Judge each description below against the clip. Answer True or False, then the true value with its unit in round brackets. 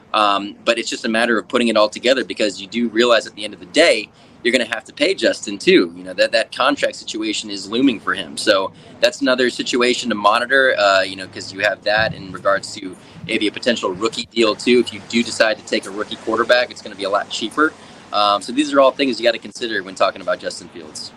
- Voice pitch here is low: True (120 Hz)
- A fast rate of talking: True (260 wpm)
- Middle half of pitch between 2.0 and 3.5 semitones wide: False (4.1 semitones)